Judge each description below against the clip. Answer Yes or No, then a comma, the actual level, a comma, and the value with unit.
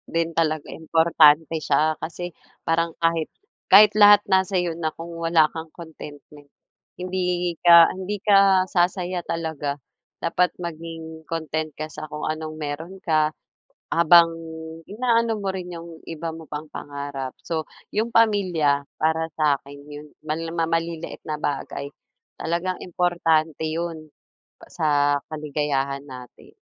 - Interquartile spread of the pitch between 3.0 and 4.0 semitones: No, narrow, 2.4 semitones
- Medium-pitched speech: Yes, medium, 160 Hz